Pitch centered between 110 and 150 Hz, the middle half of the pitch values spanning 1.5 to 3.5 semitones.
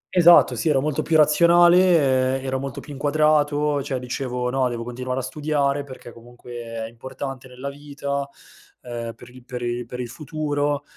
Yes: low, 135 Hz; average, 2.9 semitones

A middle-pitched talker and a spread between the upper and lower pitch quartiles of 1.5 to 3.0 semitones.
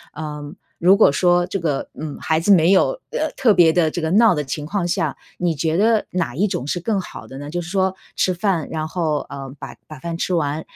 No: medium, 170 Hz; average, 3.5 semitones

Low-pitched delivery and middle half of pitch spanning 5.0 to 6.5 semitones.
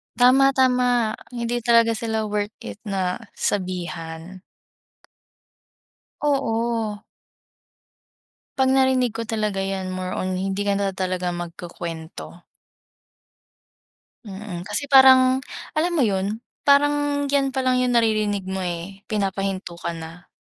No: high, 210 Hz; average, 5.3 semitones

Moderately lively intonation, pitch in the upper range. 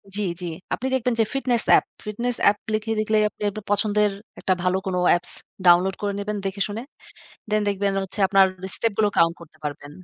No: narrow, 2.2 semitones; high, 205 Hz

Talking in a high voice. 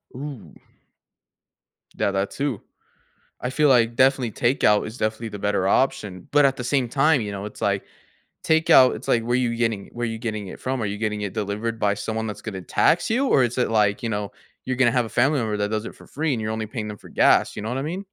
No: low, 115 Hz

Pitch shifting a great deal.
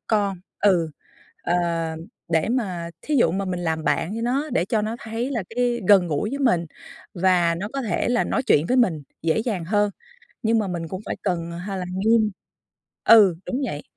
No: average, 5.0 semitones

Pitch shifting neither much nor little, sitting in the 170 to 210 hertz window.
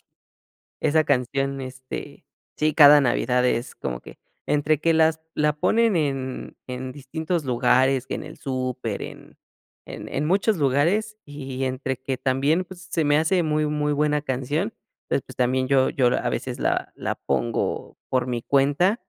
No: average, 3.1 semitones; medium, 140 Hz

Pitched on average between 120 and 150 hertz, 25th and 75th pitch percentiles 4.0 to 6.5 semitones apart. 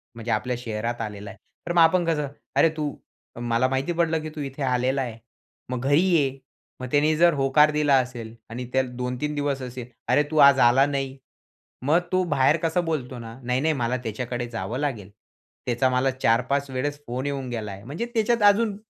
No: low, 135 Hz; average, 3.5 semitones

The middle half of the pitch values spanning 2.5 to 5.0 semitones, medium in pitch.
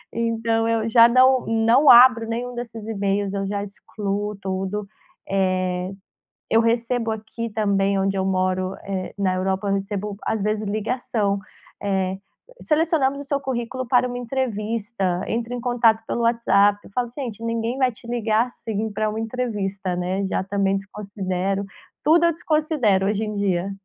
No: average, 3.3 semitones; high, 215 Hz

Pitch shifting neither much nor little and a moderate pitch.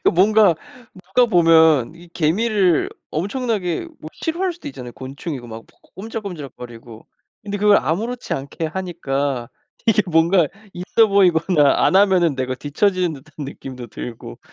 No: wide, 6.2 semitones; medium, 170 Hz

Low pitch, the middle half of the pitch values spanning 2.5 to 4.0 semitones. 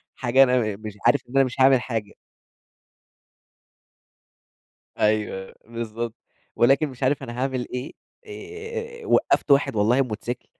Yes: low, 120 Hz; average, 3.2 semitones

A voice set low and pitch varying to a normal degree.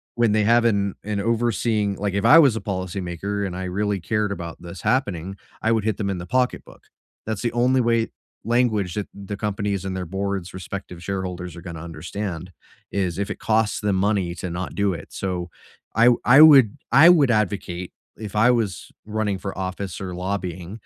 Yes: low, 100 Hz; average, 3.2 semitones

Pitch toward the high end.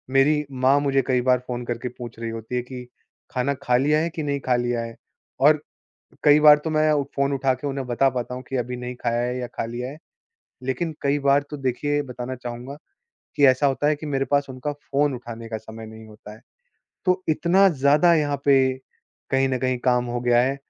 No: low, 130 Hz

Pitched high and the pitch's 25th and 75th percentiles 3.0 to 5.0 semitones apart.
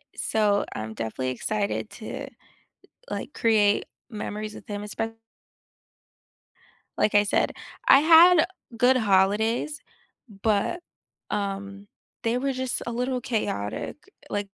Yes: high, 215 Hz; average, 3.7 semitones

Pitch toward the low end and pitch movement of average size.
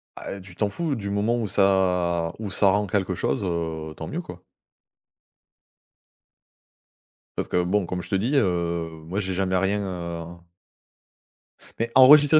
Yes: very low, 95 Hz; average, 3.0 semitones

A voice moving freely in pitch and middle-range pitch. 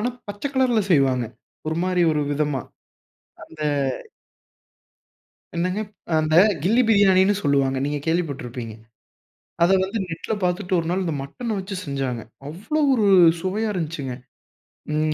Yes: wide, 5.7 semitones; medium, 170 Hz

